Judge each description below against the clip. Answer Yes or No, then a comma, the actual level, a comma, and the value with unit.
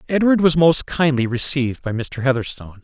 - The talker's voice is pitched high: No, medium, 140 Hz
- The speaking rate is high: No, average, 170 wpm